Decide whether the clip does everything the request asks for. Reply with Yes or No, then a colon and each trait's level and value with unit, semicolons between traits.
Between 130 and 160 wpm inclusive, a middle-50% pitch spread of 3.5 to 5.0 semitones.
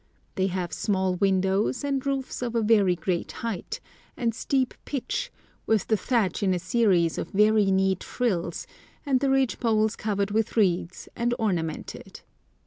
Yes: average, 155 wpm; average, 4.2 semitones